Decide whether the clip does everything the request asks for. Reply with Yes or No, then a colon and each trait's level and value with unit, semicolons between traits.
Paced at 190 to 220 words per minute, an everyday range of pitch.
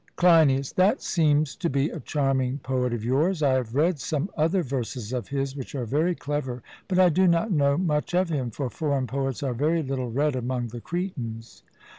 Yes: average, 200 wpm; average, 4.2 semitones